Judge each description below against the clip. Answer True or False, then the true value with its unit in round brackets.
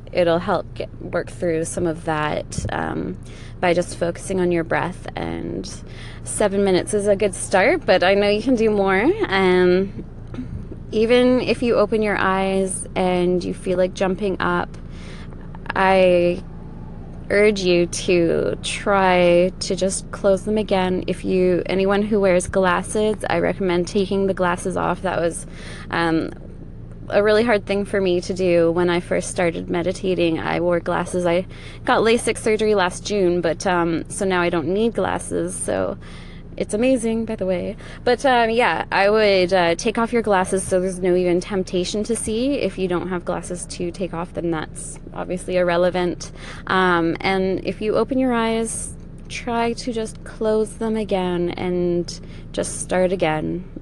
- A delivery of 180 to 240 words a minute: False (165 wpm)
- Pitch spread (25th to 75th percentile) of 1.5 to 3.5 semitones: True (2.9 semitones)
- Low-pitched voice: False (185 Hz)